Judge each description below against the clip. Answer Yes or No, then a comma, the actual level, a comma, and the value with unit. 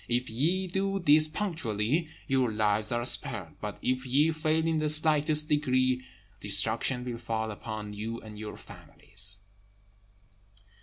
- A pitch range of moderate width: No, wide, 6.0 semitones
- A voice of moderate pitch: No, low, 125 Hz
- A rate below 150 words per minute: Yes, average, 140 wpm